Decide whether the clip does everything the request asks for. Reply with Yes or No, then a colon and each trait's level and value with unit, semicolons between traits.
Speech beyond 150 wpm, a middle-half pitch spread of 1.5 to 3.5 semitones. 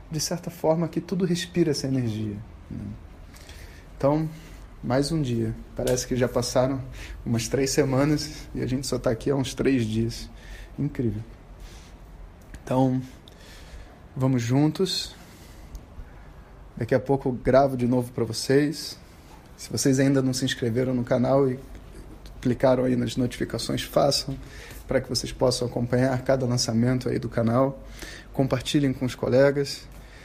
No: average, 140 wpm; average, 3.1 semitones